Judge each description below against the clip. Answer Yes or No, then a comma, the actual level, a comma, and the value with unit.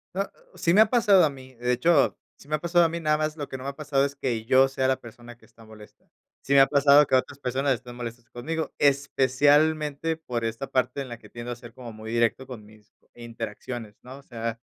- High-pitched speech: No, low, 130 Hz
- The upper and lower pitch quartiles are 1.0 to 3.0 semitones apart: No, average, 3.7 semitones